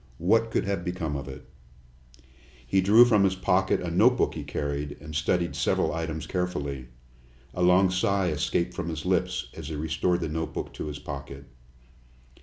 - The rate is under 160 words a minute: No, average, 170 wpm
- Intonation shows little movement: No, average, 3.5 semitones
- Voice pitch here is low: Yes, very low, 85 Hz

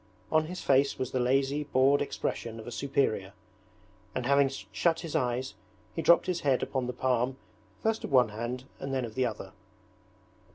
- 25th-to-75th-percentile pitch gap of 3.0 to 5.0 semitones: No, narrow, 2.4 semitones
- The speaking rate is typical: Yes, average, 180 wpm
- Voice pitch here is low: Yes, low, 130 Hz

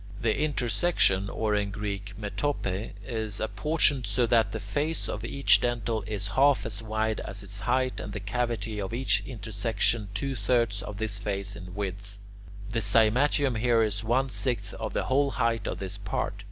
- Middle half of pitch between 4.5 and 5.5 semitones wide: No, average, 3.2 semitones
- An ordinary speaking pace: Yes, average, 180 wpm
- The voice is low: Yes, low, 110 Hz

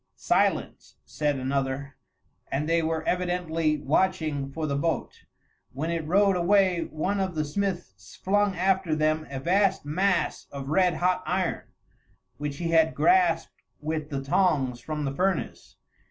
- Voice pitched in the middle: Yes, medium, 160 Hz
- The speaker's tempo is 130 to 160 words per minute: Yes, average, 145 wpm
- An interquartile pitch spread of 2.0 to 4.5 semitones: Yes, average, 4.0 semitones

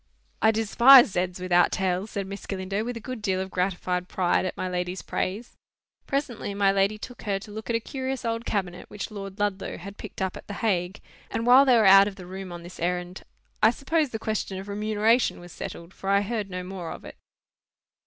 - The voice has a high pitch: Yes, high, 200 Hz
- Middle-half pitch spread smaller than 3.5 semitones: Yes, average, 3.1 semitones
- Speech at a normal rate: No, fast, 220 wpm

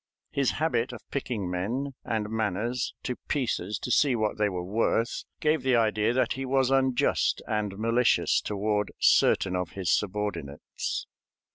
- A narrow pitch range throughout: No, average, 3.8 semitones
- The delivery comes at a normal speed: Yes, average, 150 wpm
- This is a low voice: Yes, low, 110 Hz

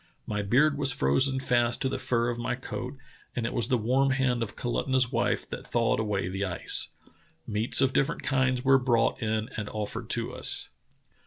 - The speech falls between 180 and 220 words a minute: Yes, average, 190 wpm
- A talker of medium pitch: No, low, 120 Hz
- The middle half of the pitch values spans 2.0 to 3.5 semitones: Yes, average, 3.1 semitones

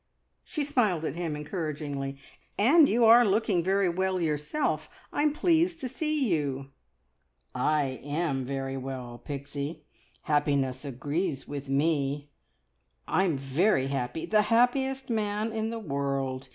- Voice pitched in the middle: Yes, medium, 155 Hz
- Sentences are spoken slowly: Yes, slow, 125 wpm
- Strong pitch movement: Yes, wide, 8.0 semitones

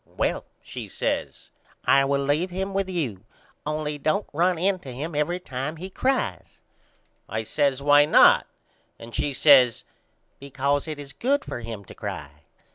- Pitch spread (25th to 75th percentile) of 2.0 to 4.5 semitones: No, average, 4.9 semitones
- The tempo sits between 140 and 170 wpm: Yes, average, 160 wpm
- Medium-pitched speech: Yes, medium, 145 Hz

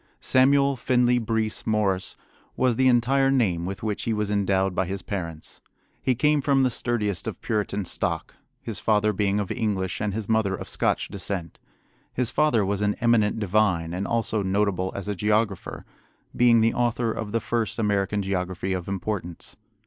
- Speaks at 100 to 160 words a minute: No, average, 170 wpm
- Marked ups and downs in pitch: No, average, 3.2 semitones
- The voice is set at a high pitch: No, low, 105 Hz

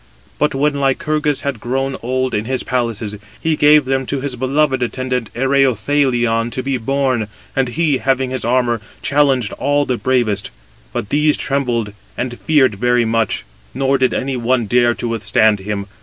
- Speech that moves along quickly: No, average, 165 wpm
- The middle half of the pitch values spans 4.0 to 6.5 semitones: No, narrow, 2.6 semitones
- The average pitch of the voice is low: Yes, low, 130 Hz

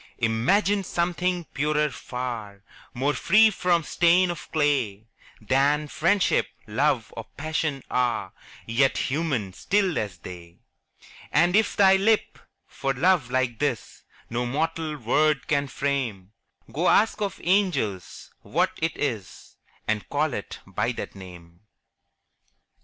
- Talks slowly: Yes, slow, 125 wpm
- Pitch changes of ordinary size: No, wide, 6.7 semitones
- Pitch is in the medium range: Yes, medium, 145 Hz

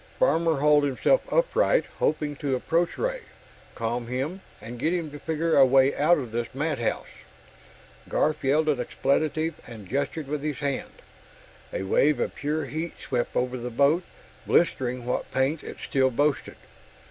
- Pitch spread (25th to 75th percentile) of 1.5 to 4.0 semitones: Yes, average, 3.7 semitones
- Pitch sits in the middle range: Yes, medium, 145 Hz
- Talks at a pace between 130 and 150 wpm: No, average, 160 wpm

